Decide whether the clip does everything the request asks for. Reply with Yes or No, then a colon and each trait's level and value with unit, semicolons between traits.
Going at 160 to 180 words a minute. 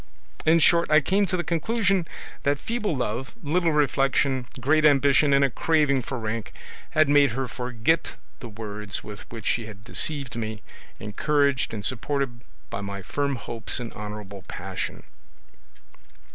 No: average, 150 wpm